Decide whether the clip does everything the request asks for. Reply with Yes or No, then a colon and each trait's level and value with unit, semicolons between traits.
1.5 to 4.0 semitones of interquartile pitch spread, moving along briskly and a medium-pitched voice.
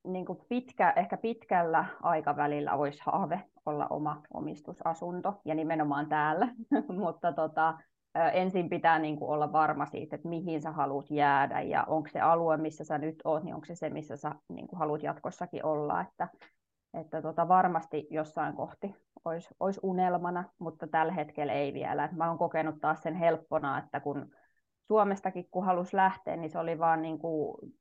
Yes: average, 2.8 semitones; fast, 170 wpm; medium, 165 Hz